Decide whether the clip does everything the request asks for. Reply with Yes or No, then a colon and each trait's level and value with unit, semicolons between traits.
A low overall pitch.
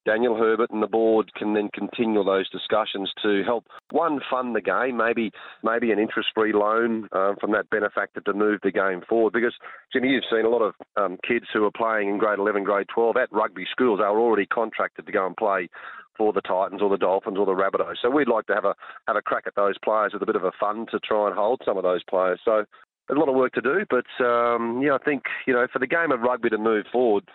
Yes: low, 110 Hz